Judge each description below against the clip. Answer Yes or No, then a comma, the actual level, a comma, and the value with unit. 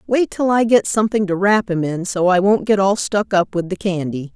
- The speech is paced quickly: Yes, fast, 260 wpm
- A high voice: Yes, high, 195 Hz